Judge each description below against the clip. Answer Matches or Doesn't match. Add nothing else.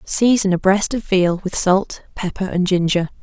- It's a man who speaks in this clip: Doesn't match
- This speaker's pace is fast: Doesn't match